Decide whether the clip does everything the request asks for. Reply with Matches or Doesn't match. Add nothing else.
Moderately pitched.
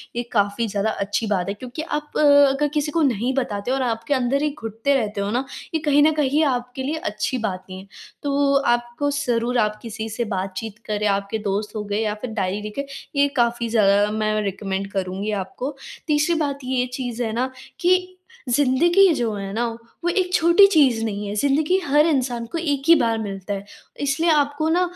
Doesn't match